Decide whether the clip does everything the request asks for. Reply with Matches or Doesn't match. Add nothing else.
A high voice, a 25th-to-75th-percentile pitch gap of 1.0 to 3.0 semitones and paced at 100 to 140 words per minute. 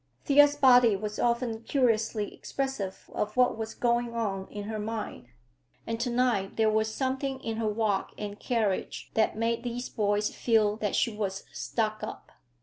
Doesn't match